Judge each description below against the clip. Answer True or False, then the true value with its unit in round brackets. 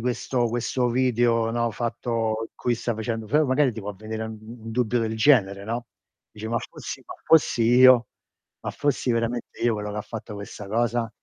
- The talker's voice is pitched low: True (115 Hz)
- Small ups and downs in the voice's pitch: True (1.8 semitones)